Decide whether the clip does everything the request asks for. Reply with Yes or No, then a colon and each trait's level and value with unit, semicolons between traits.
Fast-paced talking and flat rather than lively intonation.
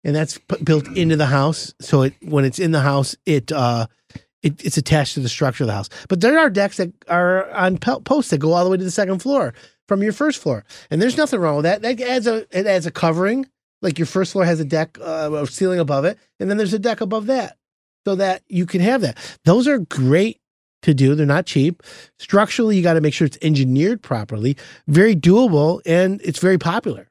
No: fast, 240 wpm; average, 5.1 semitones